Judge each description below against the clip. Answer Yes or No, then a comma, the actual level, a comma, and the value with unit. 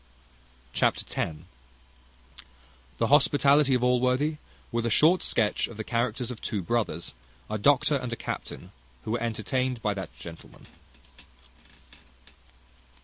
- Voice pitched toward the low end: Yes, low, 120 Hz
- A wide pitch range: No, average, 3.4 semitones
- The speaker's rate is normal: No, slow, 125 wpm